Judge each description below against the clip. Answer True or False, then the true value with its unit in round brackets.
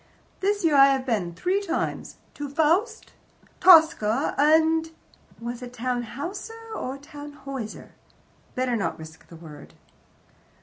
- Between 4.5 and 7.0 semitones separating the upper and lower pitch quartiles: True (5.3 semitones)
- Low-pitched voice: False (280 Hz)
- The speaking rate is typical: False (125 wpm)